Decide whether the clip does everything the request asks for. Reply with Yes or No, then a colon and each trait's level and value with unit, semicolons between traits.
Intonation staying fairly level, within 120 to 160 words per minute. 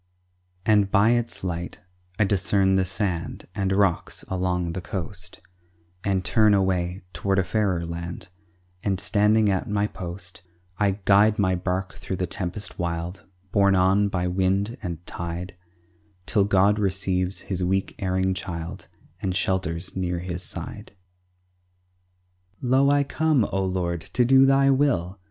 Yes: narrow, 2.3 semitones; average, 140 wpm